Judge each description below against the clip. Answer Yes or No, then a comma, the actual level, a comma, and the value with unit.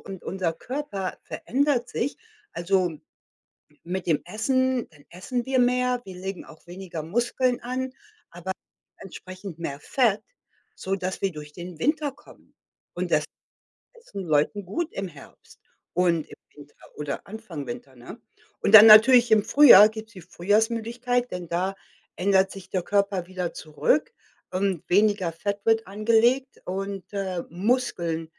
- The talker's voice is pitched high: Yes, high, 195 Hz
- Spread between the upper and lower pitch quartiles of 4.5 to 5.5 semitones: Yes, average, 5.2 semitones